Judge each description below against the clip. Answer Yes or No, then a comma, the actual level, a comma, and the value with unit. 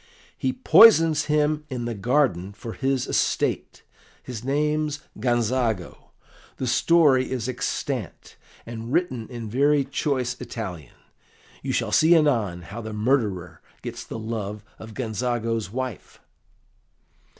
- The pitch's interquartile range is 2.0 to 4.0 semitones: No, average, 4.4 semitones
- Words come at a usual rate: No, slow, 120 wpm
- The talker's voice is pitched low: Yes, low, 125 Hz